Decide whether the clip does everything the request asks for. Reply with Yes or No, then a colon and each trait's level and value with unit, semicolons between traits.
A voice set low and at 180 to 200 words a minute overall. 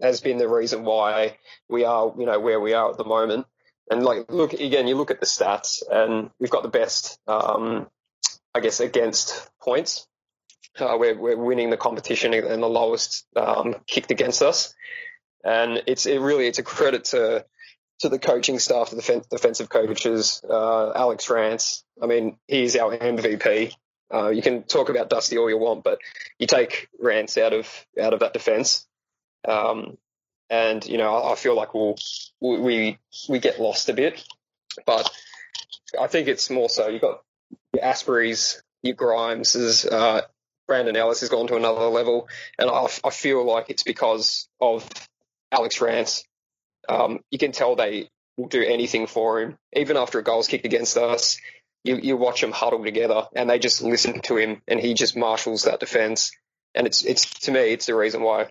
Yes: low, 120 Hz; average, 185 wpm